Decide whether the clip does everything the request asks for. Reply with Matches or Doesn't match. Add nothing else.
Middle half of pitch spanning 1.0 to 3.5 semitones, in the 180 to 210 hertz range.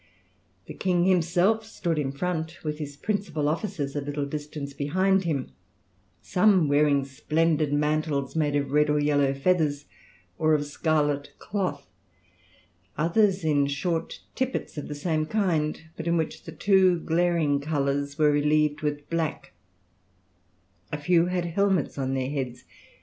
Doesn't match